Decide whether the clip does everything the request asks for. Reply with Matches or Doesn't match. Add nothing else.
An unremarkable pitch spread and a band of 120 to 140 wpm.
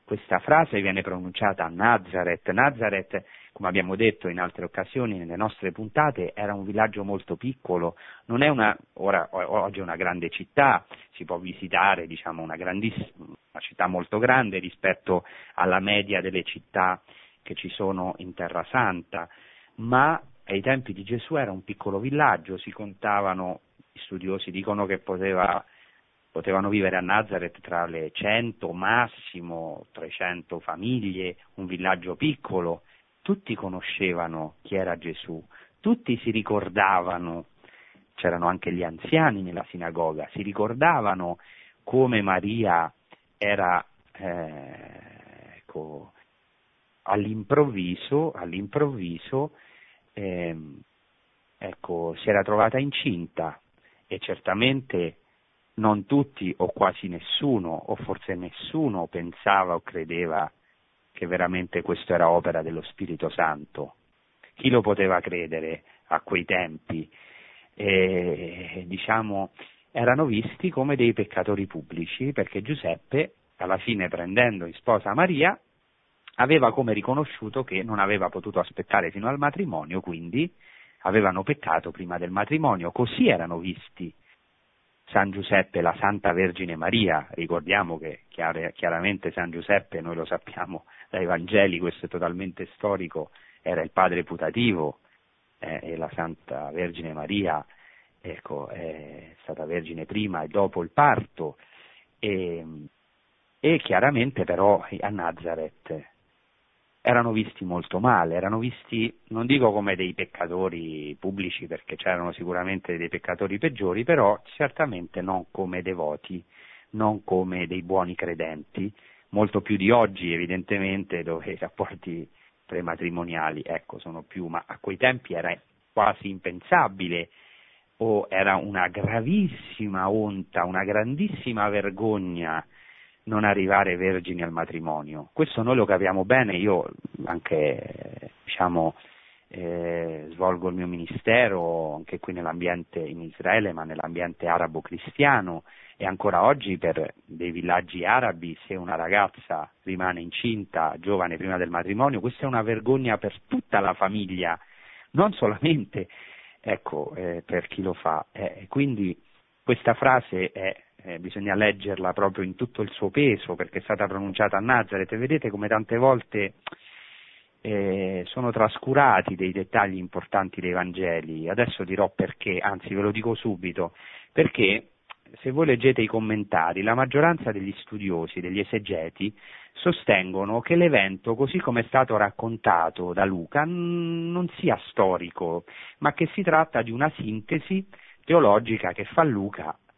Matches